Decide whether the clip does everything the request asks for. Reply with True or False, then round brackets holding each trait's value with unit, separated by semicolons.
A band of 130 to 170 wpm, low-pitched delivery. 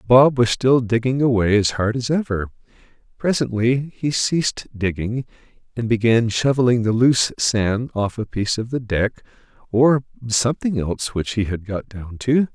True (165 wpm; 120 Hz)